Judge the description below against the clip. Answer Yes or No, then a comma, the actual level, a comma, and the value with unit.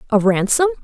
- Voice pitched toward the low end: No, very high, 250 Hz